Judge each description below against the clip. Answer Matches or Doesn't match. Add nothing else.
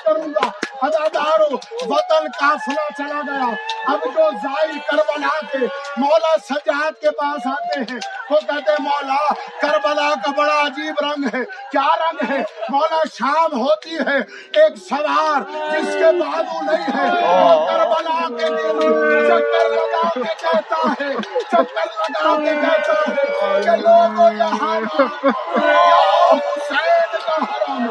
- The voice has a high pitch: Matches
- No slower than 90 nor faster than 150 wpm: Matches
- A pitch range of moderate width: Doesn't match